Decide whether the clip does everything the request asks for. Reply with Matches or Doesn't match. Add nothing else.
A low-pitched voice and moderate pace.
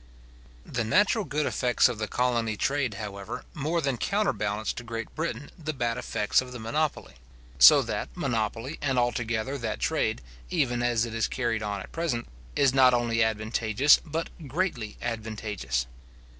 Matches